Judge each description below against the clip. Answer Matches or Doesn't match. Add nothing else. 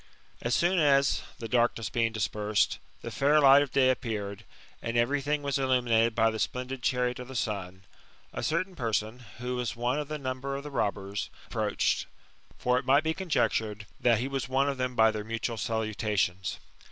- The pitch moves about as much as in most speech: Matches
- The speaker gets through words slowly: Doesn't match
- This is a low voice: Matches